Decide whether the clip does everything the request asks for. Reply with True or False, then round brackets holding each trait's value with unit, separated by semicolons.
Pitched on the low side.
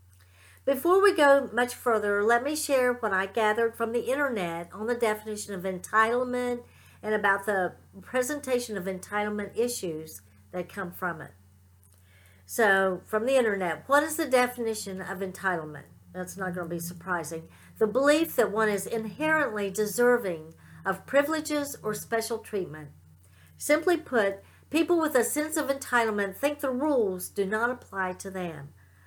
False (215 Hz)